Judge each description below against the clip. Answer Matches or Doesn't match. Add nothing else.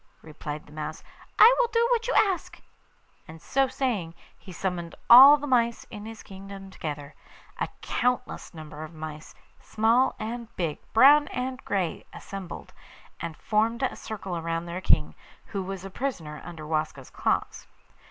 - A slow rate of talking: Doesn't match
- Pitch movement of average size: Doesn't match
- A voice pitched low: Doesn't match